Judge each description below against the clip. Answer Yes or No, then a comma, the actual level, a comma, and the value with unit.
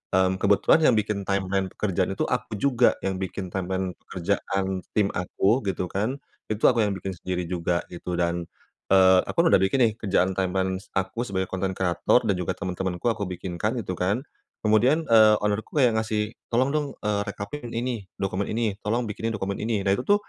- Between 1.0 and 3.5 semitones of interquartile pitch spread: Yes, average, 2.9 semitones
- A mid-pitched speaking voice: No, low, 100 Hz